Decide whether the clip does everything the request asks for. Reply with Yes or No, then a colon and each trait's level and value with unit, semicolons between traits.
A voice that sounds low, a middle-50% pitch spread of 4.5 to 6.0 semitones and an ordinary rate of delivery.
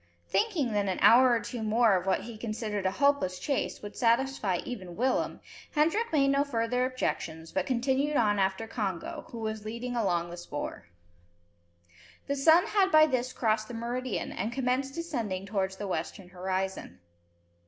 No: high, 230 Hz; wide, 5.5 semitones; average, 165 wpm